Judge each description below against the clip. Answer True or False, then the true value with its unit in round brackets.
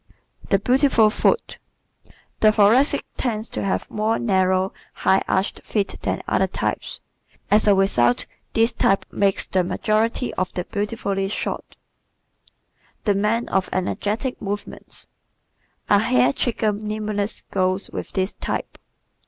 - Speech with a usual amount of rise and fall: False (2.2 semitones)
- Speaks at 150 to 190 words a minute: False (135 wpm)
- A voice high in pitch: True (205 Hz)